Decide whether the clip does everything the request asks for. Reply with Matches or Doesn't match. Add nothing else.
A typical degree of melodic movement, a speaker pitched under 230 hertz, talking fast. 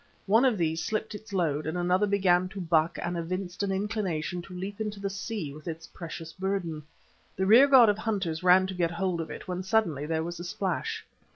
Matches